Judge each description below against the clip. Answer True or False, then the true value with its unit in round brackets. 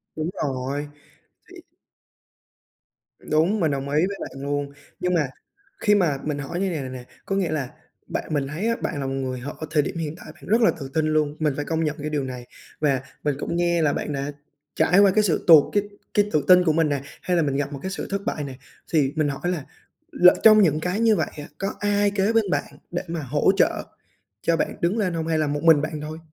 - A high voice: False (155 Hz)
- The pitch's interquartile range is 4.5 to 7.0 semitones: False (3.9 semitones)